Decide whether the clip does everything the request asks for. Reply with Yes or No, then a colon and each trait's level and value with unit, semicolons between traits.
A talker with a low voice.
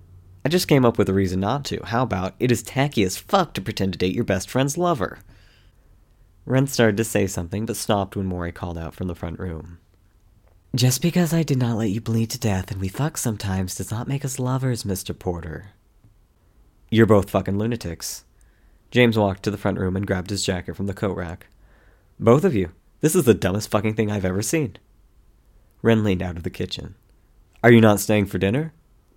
Yes: low, 100 Hz